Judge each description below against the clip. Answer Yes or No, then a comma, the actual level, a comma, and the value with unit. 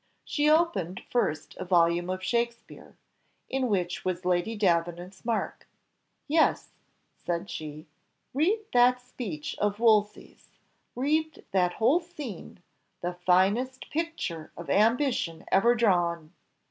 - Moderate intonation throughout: No, wide, 6.2 semitones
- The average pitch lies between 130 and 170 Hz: No, high, 205 Hz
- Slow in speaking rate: Yes, slow, 115 wpm